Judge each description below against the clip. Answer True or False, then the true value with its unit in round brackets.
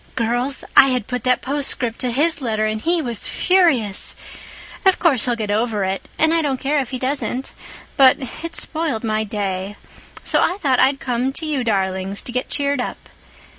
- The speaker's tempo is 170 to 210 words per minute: True (180 wpm)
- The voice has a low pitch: False (255 Hz)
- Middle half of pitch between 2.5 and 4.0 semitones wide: False (4.6 semitones)